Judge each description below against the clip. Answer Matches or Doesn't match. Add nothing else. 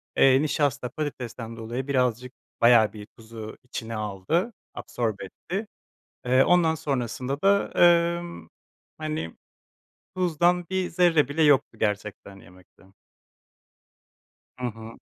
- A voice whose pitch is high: Doesn't match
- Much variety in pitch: Matches